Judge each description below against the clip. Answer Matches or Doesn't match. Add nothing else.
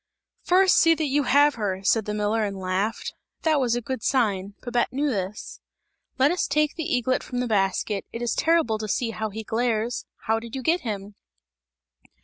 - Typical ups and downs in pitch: Matches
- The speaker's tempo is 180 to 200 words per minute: Matches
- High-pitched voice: Matches